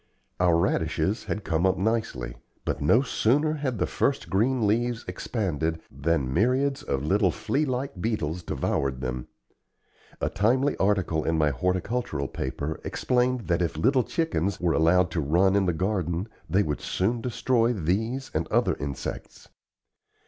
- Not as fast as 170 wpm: Yes, average, 150 wpm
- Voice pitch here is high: No, very low, 95 Hz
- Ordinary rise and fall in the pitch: No, wide, 6.8 semitones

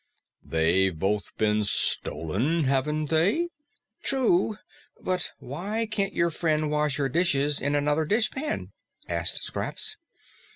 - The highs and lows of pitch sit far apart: Yes, wide, 5.9 semitones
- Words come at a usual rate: No, slow, 115 wpm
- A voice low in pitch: No, medium, 150 Hz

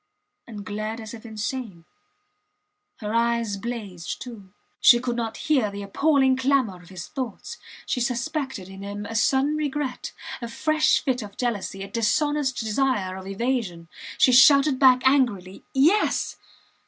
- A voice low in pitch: No, high, 235 Hz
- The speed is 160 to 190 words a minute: No, average, 145 wpm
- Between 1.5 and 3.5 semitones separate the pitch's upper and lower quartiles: No, average, 4.6 semitones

